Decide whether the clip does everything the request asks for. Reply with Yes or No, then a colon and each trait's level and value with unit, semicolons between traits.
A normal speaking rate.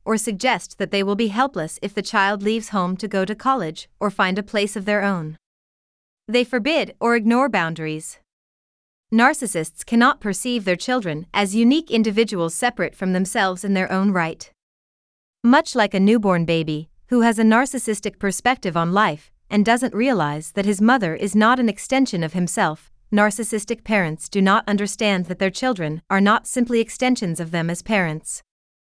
Yes: average, 170 wpm